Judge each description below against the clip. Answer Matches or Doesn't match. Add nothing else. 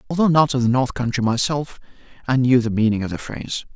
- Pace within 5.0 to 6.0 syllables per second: Doesn't match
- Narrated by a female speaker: Doesn't match